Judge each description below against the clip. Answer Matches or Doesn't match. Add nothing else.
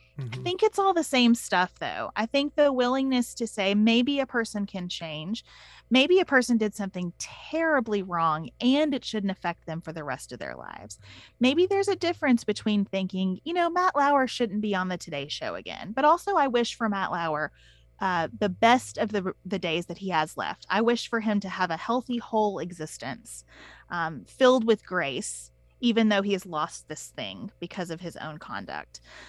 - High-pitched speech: Matches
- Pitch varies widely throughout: Matches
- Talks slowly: Doesn't match